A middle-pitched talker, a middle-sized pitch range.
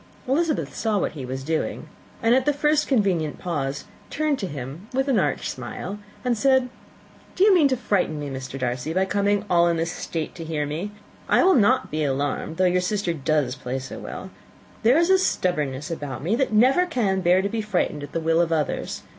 No: medium, 180 Hz; wide, 8.3 semitones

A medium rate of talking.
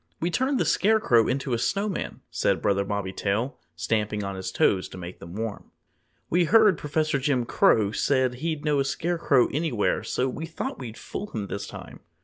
Yes: average, 185 wpm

